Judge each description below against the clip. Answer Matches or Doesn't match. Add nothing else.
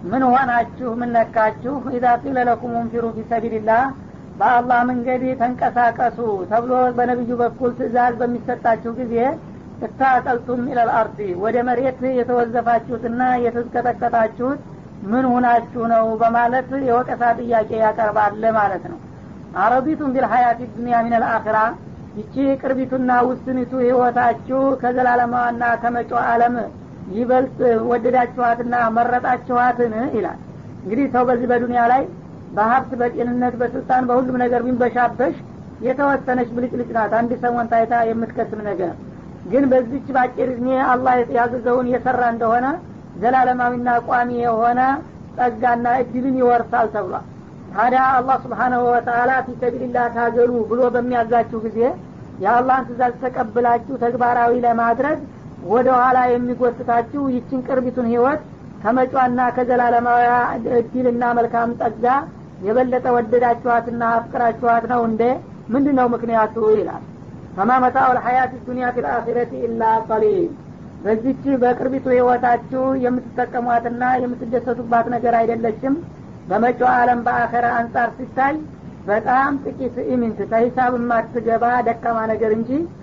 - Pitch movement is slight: Matches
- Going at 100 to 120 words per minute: Matches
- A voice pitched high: Matches